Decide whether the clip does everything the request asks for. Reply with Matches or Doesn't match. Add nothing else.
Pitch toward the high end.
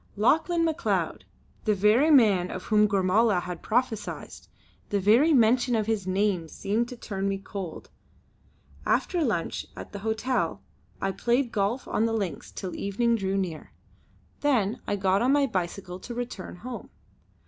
Matches